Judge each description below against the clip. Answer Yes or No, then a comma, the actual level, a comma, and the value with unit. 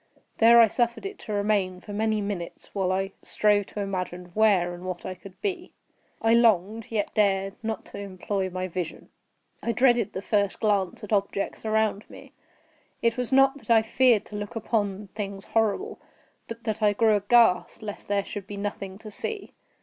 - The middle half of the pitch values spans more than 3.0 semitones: No, narrow, 2.6 semitones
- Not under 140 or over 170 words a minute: No, average, 185 wpm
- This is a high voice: Yes, high, 205 Hz